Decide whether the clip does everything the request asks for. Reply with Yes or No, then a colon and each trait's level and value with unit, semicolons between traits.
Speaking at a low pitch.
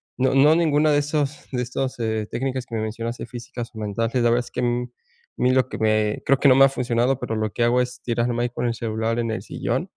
Yes: low, 120 Hz